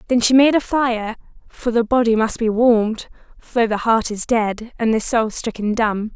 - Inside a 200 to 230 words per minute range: Yes, fast, 205 wpm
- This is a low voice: No, high, 230 Hz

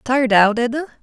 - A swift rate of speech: No, average, 175 wpm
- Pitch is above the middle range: Yes, high, 245 Hz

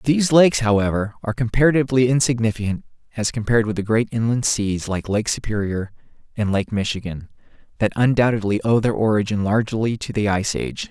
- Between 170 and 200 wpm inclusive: No, average, 160 wpm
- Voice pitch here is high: No, low, 110 Hz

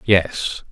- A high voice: No, very low, 90 Hz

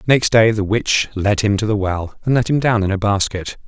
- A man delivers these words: Yes, male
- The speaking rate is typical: No, fast, 260 wpm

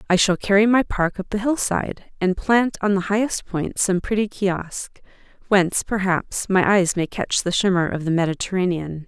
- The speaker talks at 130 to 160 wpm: No, average, 185 wpm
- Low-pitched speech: No, high, 190 Hz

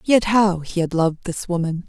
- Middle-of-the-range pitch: Yes, medium, 180 Hz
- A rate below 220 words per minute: No, fast, 225 wpm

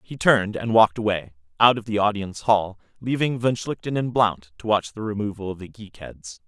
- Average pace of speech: No, fast, 215 wpm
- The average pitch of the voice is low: Yes, low, 105 Hz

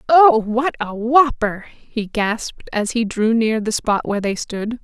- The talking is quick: No, average, 185 wpm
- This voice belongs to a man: No, female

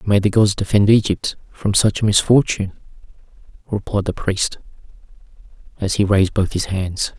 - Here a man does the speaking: Yes, male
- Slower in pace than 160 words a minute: Yes, average, 150 wpm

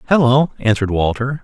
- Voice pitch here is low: Yes, low, 125 Hz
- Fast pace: No, slow, 125 wpm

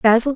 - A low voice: No, high, 240 Hz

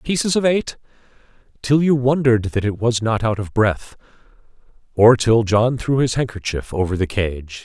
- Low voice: Yes, low, 115 Hz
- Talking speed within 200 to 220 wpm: No, average, 175 wpm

